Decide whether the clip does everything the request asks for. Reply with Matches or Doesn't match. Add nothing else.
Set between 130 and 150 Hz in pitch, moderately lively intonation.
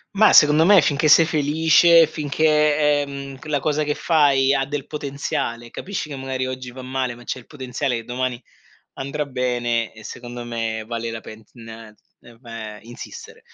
Matches